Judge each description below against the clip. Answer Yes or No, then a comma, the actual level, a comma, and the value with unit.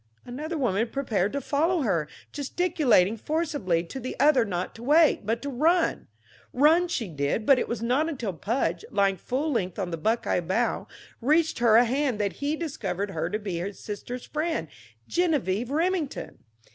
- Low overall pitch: No, high, 240 Hz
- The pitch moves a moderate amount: No, wide, 7.2 semitones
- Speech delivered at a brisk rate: No, average, 170 wpm